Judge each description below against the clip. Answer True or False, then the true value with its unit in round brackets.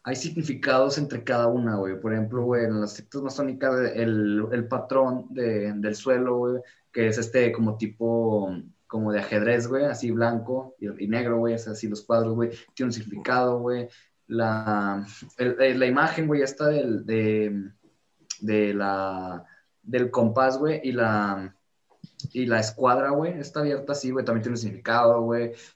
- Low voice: True (120 Hz)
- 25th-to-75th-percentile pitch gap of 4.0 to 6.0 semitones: False (3.1 semitones)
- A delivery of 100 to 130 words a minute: False (170 wpm)